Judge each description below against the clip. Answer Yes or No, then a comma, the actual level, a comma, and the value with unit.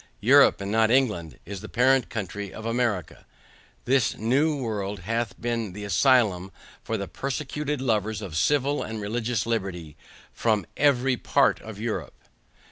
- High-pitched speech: No, low, 110 Hz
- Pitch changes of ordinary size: Yes, average, 3.9 semitones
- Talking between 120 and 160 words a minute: Yes, average, 145 wpm